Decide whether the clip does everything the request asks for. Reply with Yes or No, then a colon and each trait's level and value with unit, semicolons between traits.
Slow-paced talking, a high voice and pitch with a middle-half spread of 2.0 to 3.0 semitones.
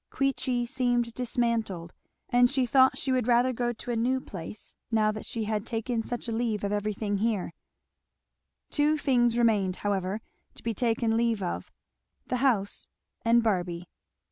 No: average, 165 wpm; high, 230 Hz; average, 2.7 semitones